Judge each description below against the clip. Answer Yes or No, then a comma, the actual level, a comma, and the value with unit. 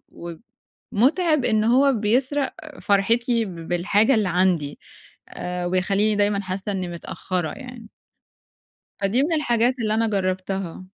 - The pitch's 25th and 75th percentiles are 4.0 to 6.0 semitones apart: Yes, average, 4.4 semitones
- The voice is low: No, high, 205 Hz